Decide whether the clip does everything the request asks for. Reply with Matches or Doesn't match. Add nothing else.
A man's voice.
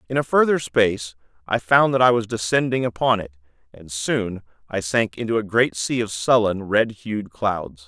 Matches